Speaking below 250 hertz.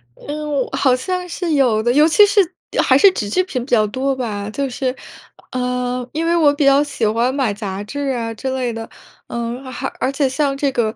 No: very high, 260 Hz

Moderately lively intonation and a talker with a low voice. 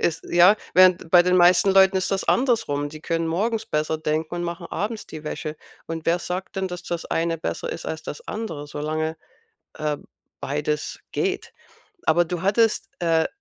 No: average, 3.2 semitones; medium, 170 Hz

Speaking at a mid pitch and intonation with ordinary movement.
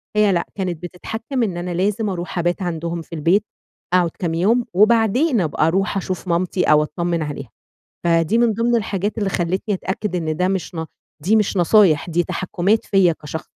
Yes: medium, 180 Hz; average, 3.7 semitones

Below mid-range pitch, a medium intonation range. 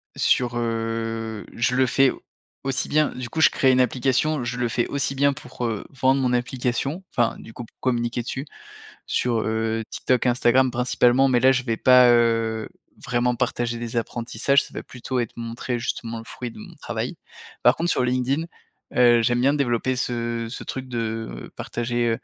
No: low, 120 Hz; narrow, 1.8 semitones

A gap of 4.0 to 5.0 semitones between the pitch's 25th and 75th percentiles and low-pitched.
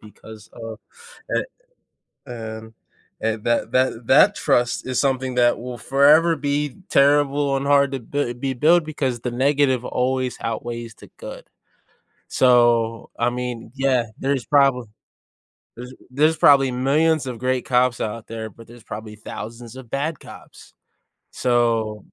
No: average, 2.9 semitones; low, 125 Hz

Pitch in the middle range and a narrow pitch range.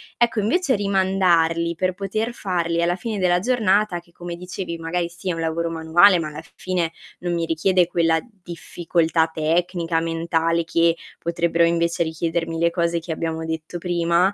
Yes: medium, 170 Hz; narrow, 1.8 semitones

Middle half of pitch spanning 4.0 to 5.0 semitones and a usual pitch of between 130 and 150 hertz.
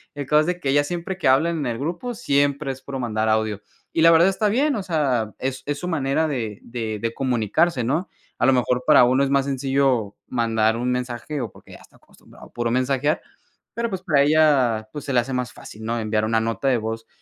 Yes: average, 4.6 semitones; low, 135 Hz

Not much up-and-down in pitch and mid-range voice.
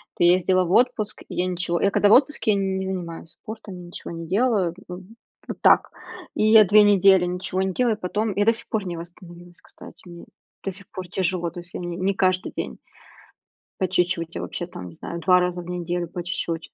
Yes: narrow, 2.3 semitones; medium, 180 Hz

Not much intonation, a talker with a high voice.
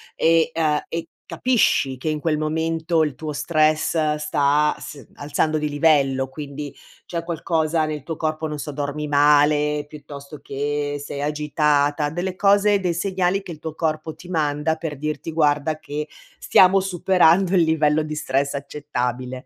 No: narrow, 1.9 semitones; medium, 150 Hz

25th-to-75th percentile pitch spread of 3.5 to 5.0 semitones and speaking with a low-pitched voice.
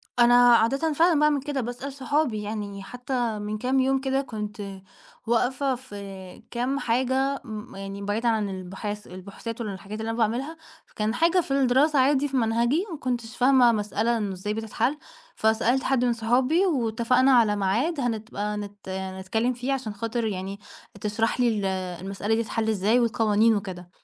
No: average, 3.9 semitones; high, 230 Hz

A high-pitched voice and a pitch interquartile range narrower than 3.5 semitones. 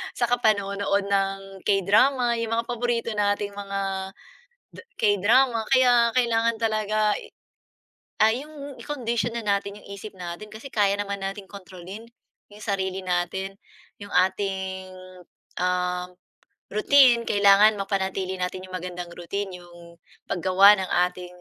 Yes: high, 200 Hz; average, 3.1 semitones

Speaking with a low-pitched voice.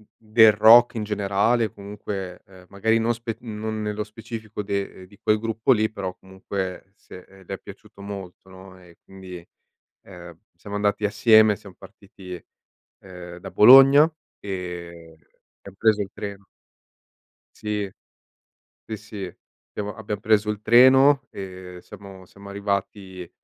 Yes: low, 100 Hz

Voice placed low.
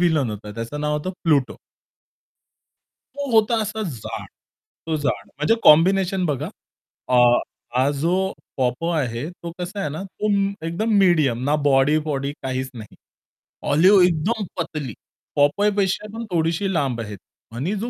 No: medium, 155 Hz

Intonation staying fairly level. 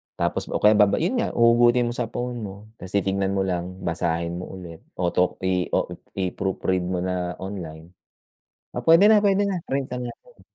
No: average, 5.1 semitones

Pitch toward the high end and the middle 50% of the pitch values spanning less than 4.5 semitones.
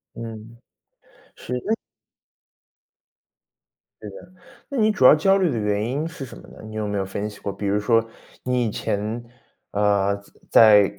No: low, 110 Hz; average, 3.9 semitones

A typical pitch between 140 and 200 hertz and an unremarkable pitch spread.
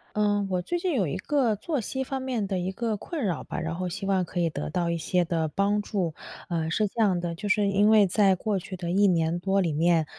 Yes: high, 195 Hz; average, 3.4 semitones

